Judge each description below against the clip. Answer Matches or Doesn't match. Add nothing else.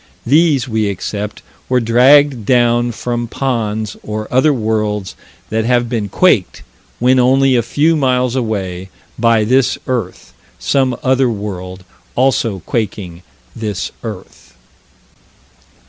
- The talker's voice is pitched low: Matches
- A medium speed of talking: Doesn't match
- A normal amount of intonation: Matches